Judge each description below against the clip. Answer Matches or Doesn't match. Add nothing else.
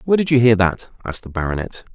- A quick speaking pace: Matches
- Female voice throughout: Doesn't match